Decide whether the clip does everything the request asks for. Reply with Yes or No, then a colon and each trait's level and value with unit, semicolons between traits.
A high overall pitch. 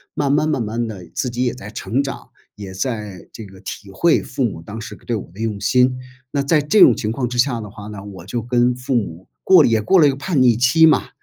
No: low, 120 Hz